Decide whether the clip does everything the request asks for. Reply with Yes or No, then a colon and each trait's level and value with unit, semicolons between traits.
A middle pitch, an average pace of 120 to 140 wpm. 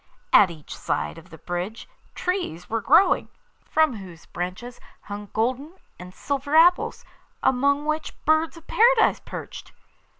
No: very high, 250 Hz; slow, 135 wpm